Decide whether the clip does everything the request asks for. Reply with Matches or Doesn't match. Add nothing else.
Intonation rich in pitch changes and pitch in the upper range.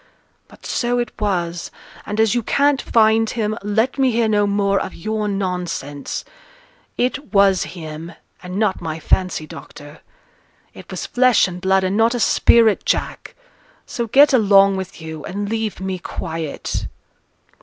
Doesn't match